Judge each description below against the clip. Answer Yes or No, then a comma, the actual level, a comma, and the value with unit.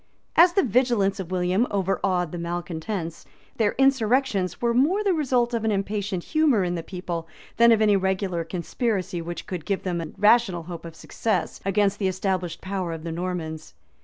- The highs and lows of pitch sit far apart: No, average, 4.6 semitones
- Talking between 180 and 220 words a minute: Yes, average, 185 wpm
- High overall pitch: Yes, high, 195 Hz